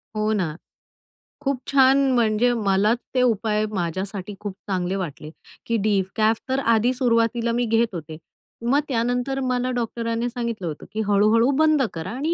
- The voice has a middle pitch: No, high, 230 Hz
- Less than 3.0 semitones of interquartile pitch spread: No, average, 3.8 semitones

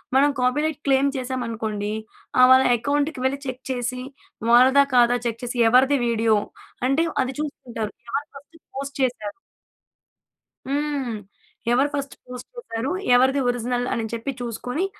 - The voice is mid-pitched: No, very high, 255 Hz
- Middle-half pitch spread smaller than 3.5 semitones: Yes, average, 2.8 semitones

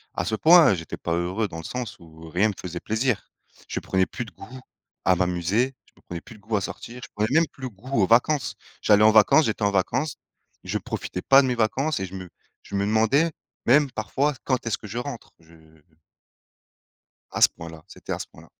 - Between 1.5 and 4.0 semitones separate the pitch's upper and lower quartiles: No, wide, 5.6 semitones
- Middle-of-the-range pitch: No, low, 110 Hz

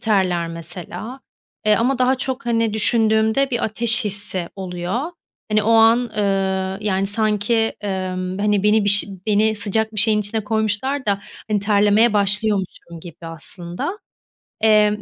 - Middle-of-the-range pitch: No, high, 210 Hz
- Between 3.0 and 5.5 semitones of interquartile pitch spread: No, narrow, 2.5 semitones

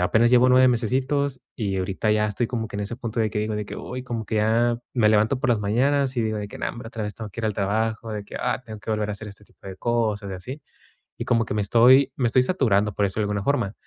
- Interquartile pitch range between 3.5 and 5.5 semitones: No, average, 3.0 semitones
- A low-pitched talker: Yes, low, 110 Hz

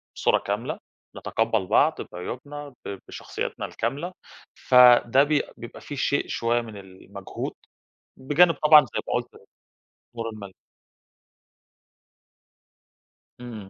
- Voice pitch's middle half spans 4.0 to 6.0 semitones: Yes, average, 5.0 semitones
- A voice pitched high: No, low, 120 Hz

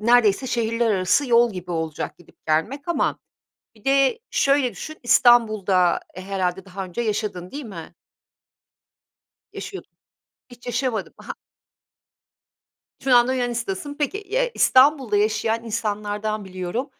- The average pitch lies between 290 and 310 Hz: No, high, 225 Hz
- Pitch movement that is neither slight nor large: Yes, average, 5.0 semitones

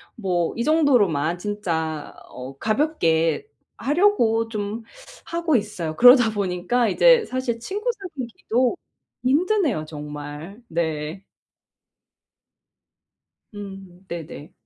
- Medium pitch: No, high, 210 Hz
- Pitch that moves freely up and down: Yes, wide, 7.8 semitones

